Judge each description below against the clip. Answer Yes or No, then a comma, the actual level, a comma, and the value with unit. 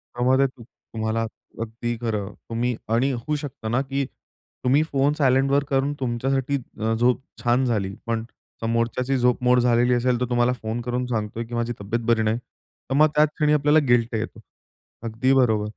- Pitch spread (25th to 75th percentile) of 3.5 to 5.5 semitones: No, narrow, 2.5 semitones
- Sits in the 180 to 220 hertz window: No, low, 120 Hz